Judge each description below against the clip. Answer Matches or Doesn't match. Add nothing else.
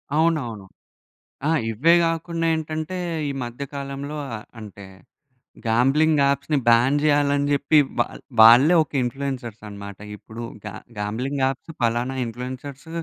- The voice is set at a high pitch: Doesn't match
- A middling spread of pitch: Matches